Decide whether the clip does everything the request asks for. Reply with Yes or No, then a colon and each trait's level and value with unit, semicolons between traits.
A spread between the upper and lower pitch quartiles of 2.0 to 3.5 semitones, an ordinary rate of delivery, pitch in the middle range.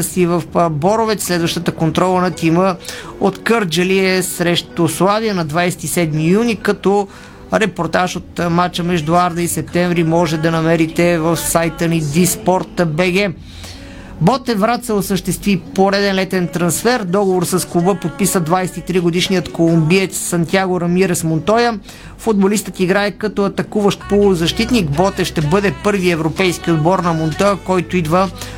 Yes: narrow, 2.5 semitones; average, 125 wpm; medium, 180 Hz